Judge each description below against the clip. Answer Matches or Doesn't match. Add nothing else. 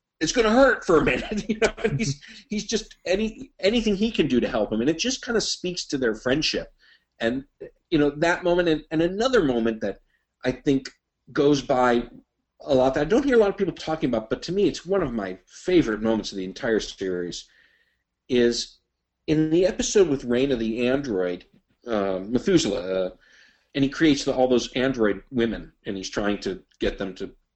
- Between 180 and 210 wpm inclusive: Matches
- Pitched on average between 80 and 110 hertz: Doesn't match